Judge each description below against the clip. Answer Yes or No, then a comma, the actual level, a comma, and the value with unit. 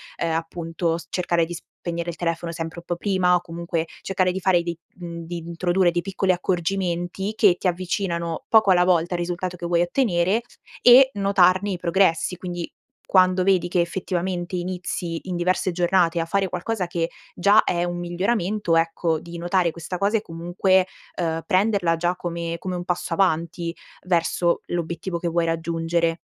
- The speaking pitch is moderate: Yes, medium, 175 Hz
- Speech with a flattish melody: Yes, narrow, 1.7 semitones